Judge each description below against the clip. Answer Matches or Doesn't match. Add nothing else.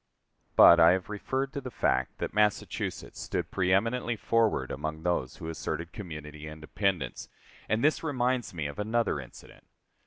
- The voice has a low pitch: Matches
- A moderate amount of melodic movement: Doesn't match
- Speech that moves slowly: Doesn't match